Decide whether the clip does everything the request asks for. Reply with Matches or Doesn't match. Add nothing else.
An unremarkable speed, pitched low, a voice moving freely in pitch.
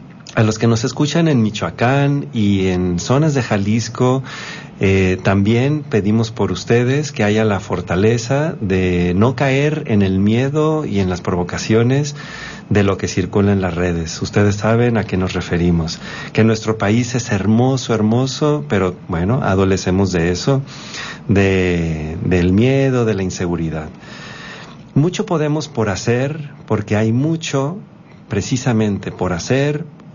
Matches